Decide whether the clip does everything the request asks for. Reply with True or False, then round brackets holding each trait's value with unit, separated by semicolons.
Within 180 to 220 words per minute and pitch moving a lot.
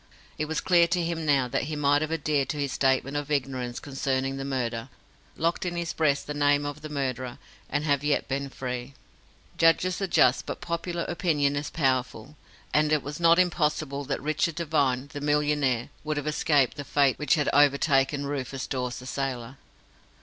False (185 wpm; 2.4 semitones)